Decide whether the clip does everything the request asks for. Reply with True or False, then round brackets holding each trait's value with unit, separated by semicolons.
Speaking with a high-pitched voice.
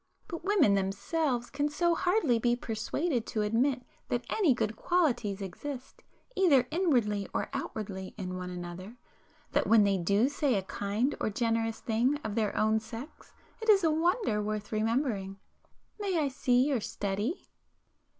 True (235 Hz)